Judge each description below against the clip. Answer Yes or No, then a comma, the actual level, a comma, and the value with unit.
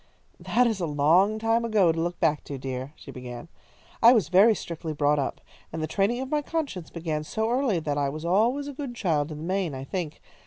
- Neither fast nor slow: No, fast, 230 wpm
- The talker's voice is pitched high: No, medium, 175 Hz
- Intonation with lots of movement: Yes, wide, 7.1 semitones